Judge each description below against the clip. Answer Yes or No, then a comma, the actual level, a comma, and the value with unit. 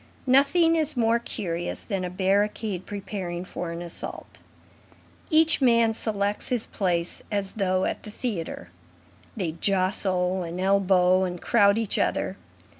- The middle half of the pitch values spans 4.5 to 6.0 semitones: No, average, 3.8 semitones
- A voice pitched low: No, high, 195 Hz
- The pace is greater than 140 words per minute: No, slow, 135 wpm